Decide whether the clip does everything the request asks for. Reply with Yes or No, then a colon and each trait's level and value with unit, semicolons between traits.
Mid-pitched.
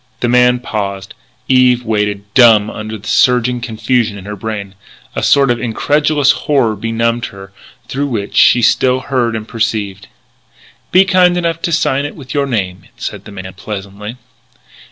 No: low, 115 Hz